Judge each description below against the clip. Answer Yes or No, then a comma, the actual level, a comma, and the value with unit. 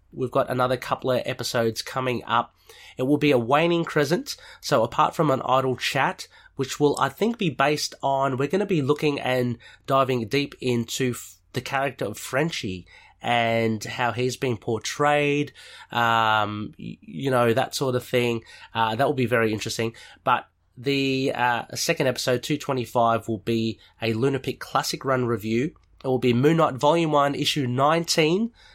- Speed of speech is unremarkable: Yes, average, 170 wpm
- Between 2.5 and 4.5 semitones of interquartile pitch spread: Yes, average, 3.5 semitones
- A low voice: Yes, low, 130 Hz